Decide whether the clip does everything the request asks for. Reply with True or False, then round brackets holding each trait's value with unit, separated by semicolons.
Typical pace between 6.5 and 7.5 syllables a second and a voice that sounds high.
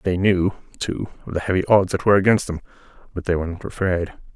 False (6.9 syllables/s; 95 Hz)